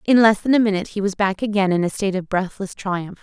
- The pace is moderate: No, fast, 280 wpm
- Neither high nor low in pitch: No, high, 200 Hz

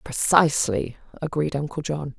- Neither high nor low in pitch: Yes, medium, 145 Hz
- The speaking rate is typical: No, slow, 110 wpm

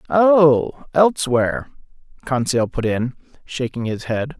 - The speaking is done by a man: Yes, male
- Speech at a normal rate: No, slow, 110 wpm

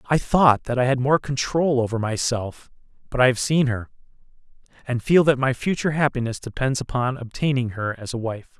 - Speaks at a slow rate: No, average, 190 wpm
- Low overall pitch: Yes, low, 130 Hz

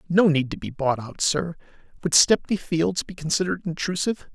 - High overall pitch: No, medium, 165 Hz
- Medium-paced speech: Yes, average, 180 wpm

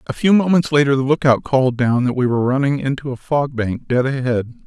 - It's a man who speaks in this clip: Yes, male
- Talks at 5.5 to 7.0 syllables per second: Yes, 5.9 syllables/s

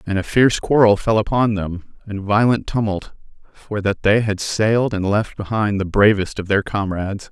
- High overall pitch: No, low, 105 Hz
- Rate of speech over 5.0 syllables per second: No, 4.9 syllables/s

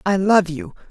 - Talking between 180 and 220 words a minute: Yes, average, 200 wpm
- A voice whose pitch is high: No, medium, 180 Hz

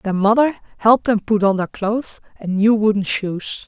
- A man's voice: No, female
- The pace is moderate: Yes, average, 195 wpm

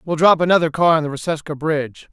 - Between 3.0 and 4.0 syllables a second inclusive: No, 6.5 syllables/s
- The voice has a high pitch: No, medium, 155 Hz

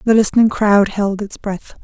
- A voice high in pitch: Yes, high, 205 Hz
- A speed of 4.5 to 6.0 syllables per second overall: Yes, 4.8 syllables/s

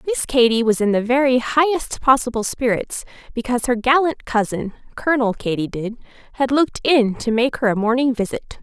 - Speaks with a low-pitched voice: No, high, 245 Hz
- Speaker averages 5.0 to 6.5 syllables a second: Yes, 5.4 syllables/s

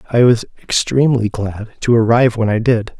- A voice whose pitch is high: No, low, 115 Hz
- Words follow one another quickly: No, average, 180 wpm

